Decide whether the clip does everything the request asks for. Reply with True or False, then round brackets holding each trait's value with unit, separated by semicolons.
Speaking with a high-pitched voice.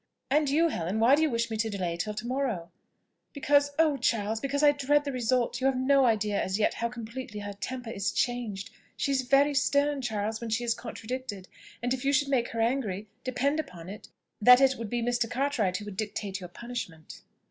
True (240 Hz)